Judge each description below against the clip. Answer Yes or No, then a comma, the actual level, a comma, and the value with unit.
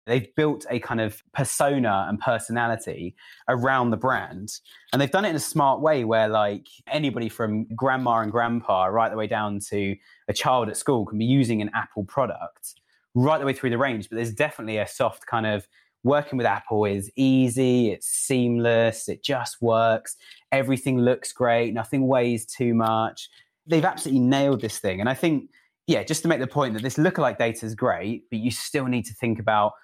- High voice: No, low, 120 Hz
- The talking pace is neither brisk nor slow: Yes, average, 195 wpm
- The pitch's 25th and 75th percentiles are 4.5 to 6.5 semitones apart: No, average, 3.3 semitones